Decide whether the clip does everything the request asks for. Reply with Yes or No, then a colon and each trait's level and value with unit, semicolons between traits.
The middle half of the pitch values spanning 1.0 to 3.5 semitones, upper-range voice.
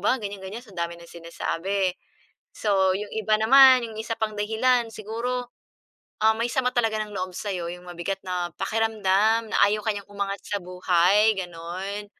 Yes: average, 3.1 semitones; high, 205 Hz